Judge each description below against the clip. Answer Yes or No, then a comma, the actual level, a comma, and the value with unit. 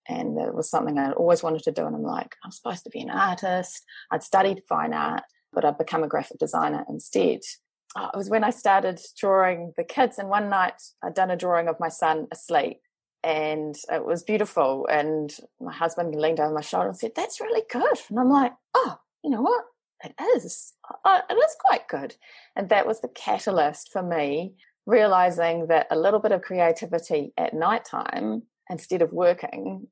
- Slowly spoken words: No, average, 195 wpm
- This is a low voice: No, medium, 185 Hz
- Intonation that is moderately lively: No, wide, 6.4 semitones